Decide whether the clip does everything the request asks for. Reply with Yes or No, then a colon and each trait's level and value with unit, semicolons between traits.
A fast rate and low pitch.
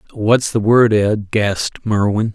No: average, 155 wpm; low, 105 Hz